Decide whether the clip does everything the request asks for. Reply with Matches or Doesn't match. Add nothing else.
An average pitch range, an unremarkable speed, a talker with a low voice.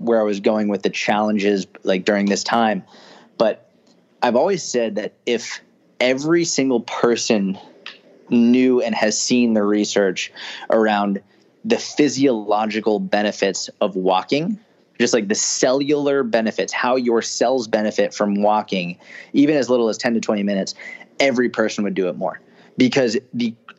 Matches